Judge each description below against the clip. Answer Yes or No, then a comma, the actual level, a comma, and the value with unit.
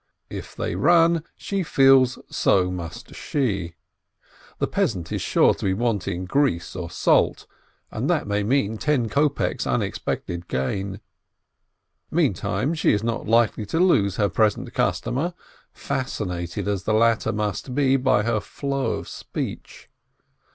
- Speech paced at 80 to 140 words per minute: Yes, slow, 135 wpm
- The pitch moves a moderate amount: No, wide, 5.8 semitones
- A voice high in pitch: No, low, 110 Hz